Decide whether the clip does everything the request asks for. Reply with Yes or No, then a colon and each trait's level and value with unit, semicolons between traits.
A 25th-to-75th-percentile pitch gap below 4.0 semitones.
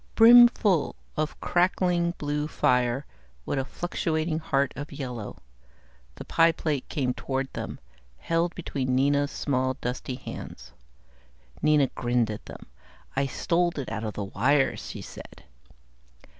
No: average, 4.4 semitones